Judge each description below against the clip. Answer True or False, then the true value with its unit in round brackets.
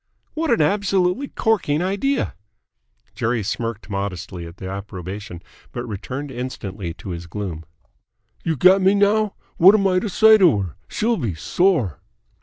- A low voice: True (125 Hz)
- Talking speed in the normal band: True (150 wpm)